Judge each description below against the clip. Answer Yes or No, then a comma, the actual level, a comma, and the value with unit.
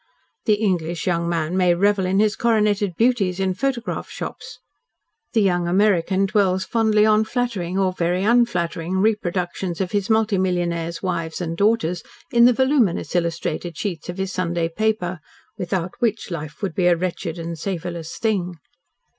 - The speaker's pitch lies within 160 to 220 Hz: Yes, medium, 185 Hz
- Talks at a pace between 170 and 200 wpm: No, average, 155 wpm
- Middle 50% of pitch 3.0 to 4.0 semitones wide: Yes, average, 3.5 semitones